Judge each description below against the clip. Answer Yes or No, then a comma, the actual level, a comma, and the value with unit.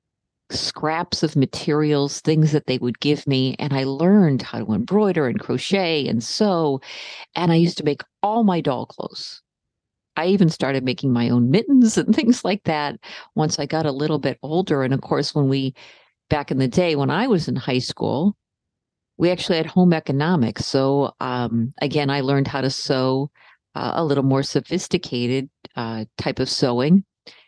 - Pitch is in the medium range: Yes, medium, 145 Hz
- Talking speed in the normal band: Yes, average, 180 wpm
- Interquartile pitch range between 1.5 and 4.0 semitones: No, average, 4.4 semitones